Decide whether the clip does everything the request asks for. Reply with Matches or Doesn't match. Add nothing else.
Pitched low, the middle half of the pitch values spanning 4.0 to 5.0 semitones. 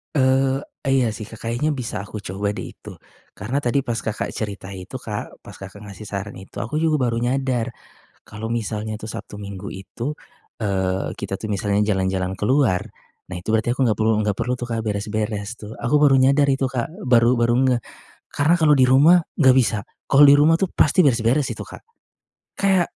Matches